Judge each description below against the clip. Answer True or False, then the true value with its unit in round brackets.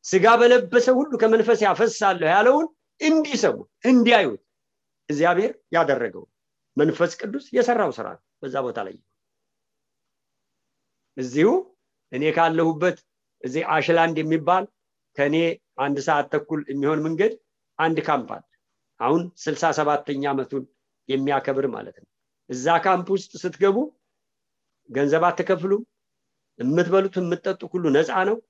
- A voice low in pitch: False (180 Hz)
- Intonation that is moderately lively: False (6.9 semitones)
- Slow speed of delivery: True (105 wpm)